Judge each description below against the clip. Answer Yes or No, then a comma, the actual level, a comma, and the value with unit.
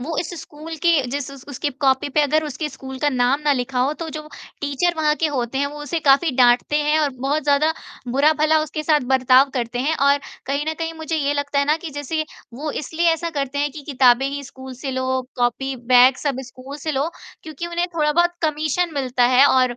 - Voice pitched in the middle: No, very high, 285 Hz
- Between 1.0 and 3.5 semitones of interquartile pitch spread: Yes, average, 2.8 semitones